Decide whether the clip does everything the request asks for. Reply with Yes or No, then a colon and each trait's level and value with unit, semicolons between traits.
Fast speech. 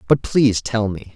Yes: fast, 210 wpm